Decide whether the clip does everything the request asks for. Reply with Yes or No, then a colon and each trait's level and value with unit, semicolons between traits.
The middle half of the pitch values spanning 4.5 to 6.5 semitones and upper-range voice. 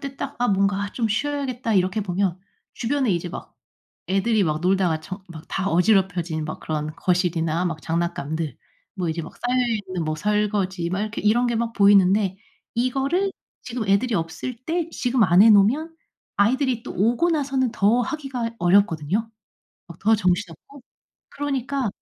Yes: wide, 5.5 semitones; high, 205 Hz